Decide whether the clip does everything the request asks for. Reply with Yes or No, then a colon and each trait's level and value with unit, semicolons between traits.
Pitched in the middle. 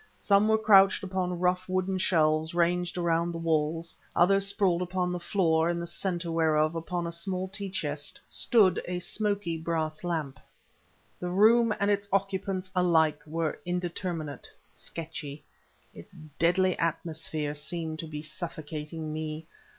Yes: medium, 170 Hz